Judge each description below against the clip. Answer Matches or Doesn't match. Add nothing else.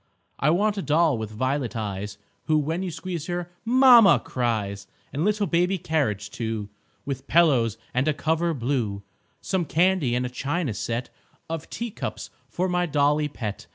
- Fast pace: Doesn't match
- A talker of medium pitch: Matches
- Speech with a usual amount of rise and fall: Doesn't match